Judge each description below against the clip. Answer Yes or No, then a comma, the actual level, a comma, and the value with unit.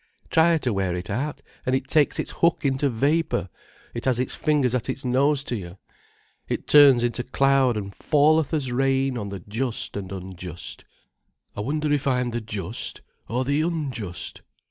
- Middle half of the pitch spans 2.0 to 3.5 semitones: No, average, 4.8 semitones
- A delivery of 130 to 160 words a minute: No, average, 175 wpm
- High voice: No, low, 130 Hz